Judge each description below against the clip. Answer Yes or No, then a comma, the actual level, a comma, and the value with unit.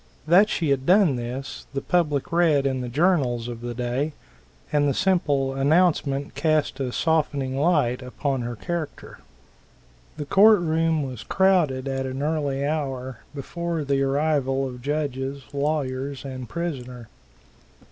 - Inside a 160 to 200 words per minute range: No, average, 140 wpm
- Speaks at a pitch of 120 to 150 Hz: Yes, medium, 140 Hz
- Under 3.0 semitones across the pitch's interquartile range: No, average, 3.3 semitones